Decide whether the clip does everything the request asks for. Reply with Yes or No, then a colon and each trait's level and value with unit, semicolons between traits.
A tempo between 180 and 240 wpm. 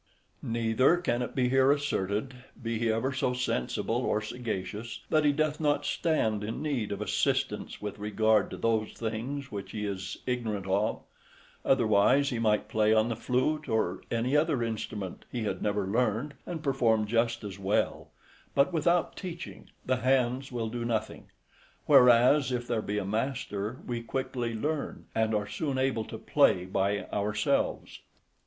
No: average, 160 wpm